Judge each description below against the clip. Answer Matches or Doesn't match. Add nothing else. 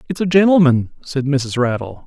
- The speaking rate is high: Doesn't match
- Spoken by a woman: Doesn't match